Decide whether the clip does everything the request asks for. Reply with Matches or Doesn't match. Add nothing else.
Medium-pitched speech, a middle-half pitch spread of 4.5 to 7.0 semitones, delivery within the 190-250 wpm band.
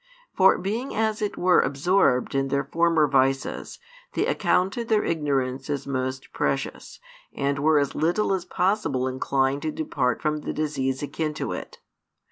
Doesn't match